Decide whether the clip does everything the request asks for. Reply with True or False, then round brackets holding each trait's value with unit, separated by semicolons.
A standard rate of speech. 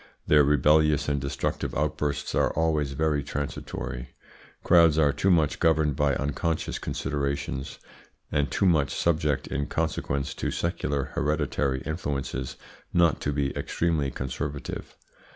False (125 wpm)